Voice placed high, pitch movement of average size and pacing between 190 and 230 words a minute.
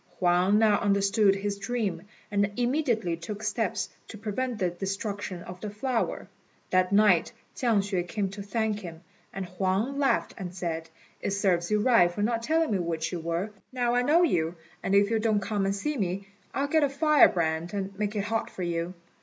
Yes: high, 200 Hz; average, 3.7 semitones; average, 195 wpm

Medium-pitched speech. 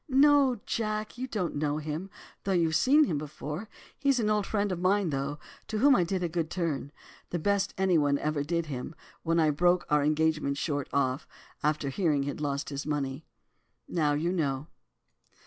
Yes: medium, 160 Hz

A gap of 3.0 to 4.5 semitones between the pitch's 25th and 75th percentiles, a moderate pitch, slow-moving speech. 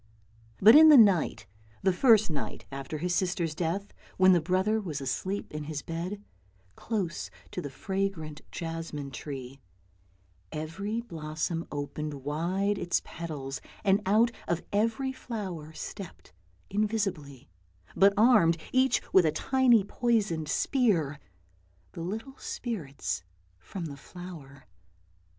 No: average, 5.2 semitones; medium, 175 Hz; slow, 125 wpm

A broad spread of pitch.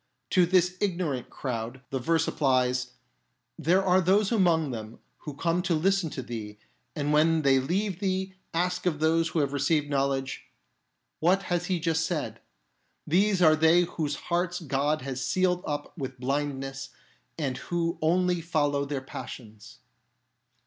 No: average, 4.7 semitones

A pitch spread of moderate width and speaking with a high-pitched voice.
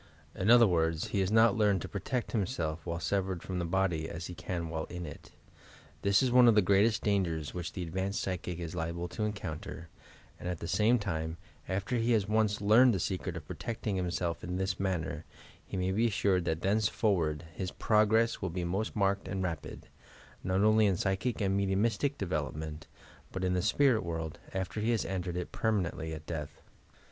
No: average, 3.8 semitones; very low, 95 Hz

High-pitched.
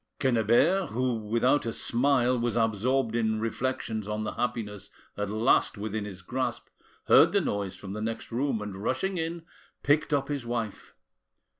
No: low, 115 Hz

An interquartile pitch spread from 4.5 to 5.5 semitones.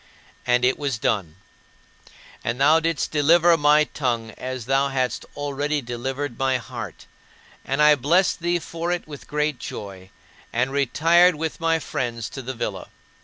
No: average, 3.8 semitones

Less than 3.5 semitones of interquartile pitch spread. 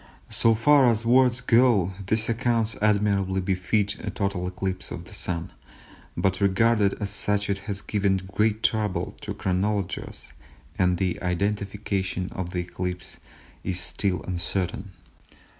Yes: average, 2.7 semitones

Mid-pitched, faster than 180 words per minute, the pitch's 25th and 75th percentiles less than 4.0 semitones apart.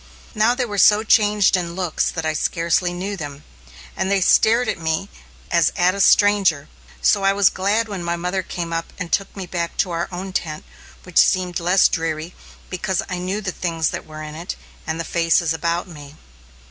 Yes: medium, 180 Hz; average, 200 wpm; average, 2.9 semitones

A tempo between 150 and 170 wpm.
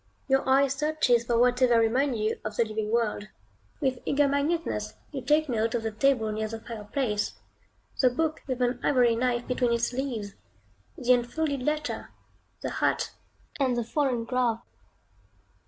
Yes: average, 160 wpm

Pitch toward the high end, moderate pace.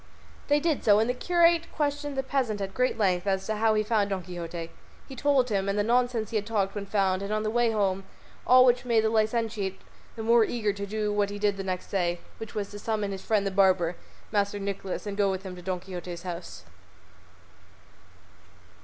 No: high, 205 Hz; fast, 225 wpm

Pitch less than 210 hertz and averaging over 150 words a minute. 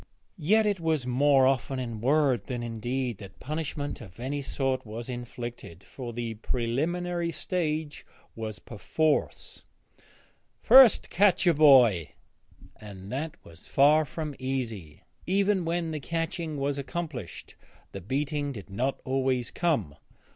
No: low, 135 Hz; slow, 135 wpm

